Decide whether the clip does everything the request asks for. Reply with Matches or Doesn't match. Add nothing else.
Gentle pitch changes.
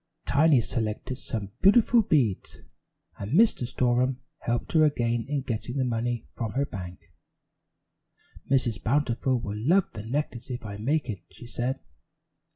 Doesn't match